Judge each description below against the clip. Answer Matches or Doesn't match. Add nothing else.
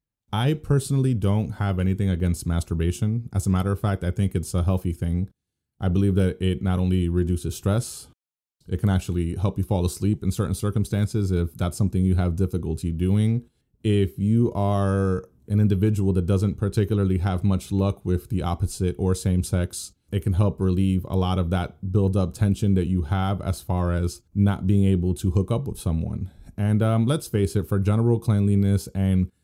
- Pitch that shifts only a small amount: Matches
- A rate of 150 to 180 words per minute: Doesn't match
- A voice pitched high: Doesn't match